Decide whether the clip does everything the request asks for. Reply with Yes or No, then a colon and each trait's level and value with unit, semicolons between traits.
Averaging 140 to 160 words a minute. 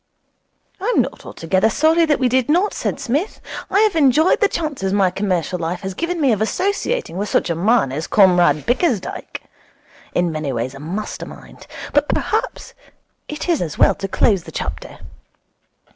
No: average, 175 wpm